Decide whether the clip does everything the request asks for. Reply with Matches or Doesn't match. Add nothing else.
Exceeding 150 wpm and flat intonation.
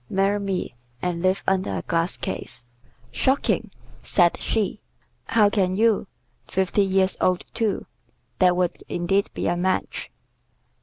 Doesn't match